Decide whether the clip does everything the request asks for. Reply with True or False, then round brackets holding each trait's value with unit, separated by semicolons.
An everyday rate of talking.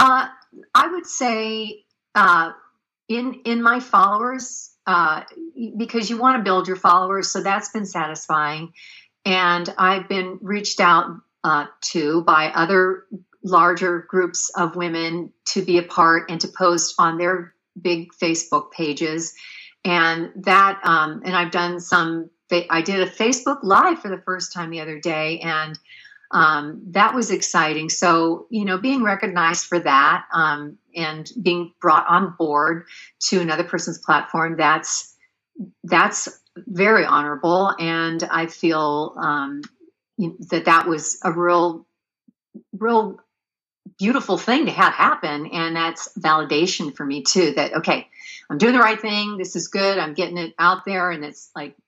True (150 wpm)